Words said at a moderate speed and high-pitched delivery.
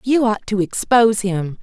Yes: average, 185 wpm; high, 210 Hz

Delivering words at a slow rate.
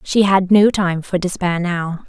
No: average, 200 wpm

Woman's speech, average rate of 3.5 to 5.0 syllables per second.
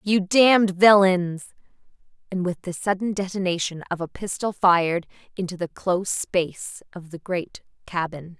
Yes: female; 4.7 syllables/s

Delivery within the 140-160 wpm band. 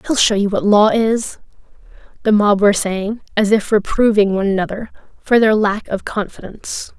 No: average, 170 wpm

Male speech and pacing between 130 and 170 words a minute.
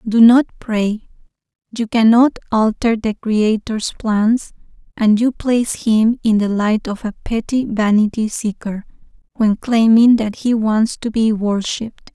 No: female; average, 145 wpm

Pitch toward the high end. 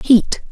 Yes: high, 230 Hz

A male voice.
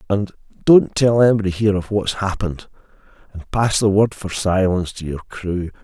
Yes: male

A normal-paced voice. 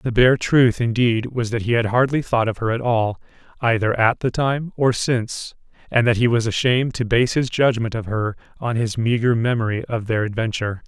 No: fast, 210 wpm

